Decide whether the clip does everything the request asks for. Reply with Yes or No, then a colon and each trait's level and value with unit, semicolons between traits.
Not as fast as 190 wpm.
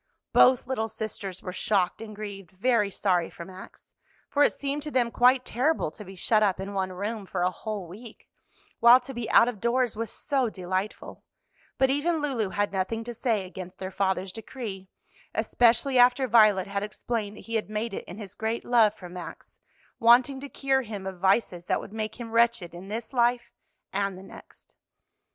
No: average, 195 wpm